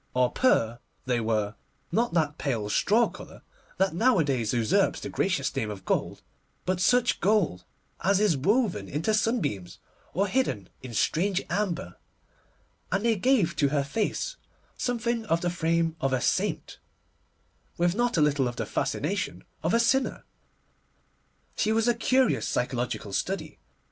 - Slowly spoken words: No, average, 145 wpm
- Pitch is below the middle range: No, medium, 170 Hz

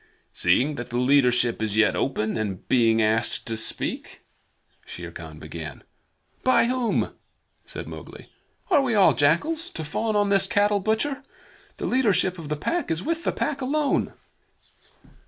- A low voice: No, medium, 160 Hz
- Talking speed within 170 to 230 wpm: No, average, 155 wpm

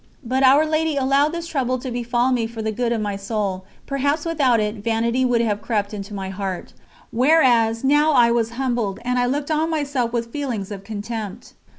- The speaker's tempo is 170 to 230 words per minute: Yes, average, 200 wpm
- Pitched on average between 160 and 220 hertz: No, high, 240 Hz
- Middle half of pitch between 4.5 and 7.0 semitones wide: No, average, 4.0 semitones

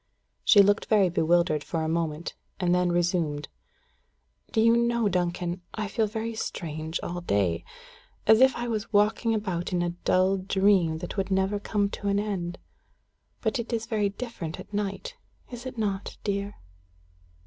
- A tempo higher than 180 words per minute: No, average, 165 wpm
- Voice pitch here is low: No, high, 195 Hz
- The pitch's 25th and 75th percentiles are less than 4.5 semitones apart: Yes, average, 3.8 semitones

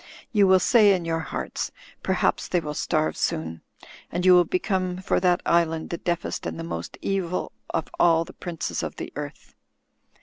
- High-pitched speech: No, medium, 175 Hz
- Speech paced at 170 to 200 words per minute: Yes, average, 180 wpm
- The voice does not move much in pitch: Yes, narrow, 2.1 semitones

